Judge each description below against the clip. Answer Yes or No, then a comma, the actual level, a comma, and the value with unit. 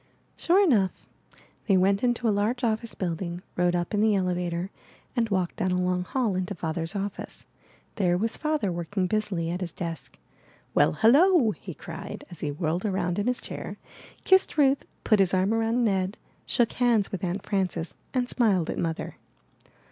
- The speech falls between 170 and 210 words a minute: Yes, average, 180 wpm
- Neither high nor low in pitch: No, high, 195 Hz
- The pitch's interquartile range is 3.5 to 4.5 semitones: Yes, average, 4.2 semitones